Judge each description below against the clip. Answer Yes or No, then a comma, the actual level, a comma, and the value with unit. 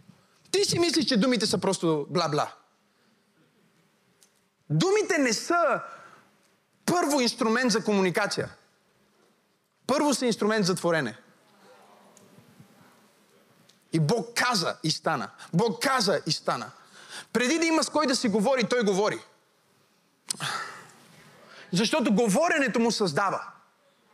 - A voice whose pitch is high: Yes, high, 210 Hz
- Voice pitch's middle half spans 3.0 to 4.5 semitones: No, average, 5.0 semitones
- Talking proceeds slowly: Yes, slow, 105 wpm